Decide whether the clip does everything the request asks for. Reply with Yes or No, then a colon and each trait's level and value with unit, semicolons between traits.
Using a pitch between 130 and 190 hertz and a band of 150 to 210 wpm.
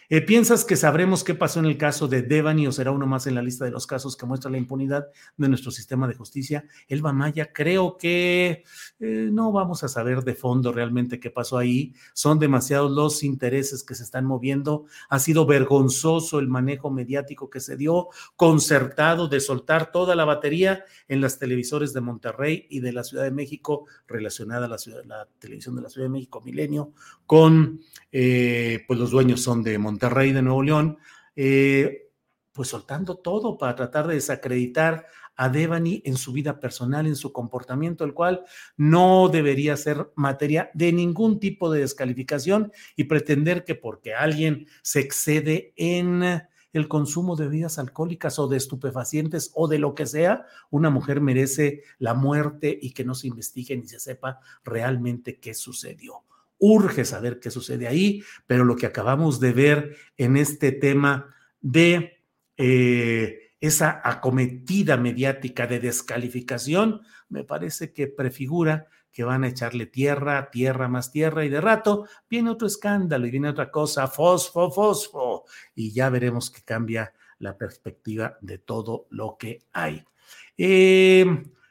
Yes: medium, 140 Hz; average, 165 wpm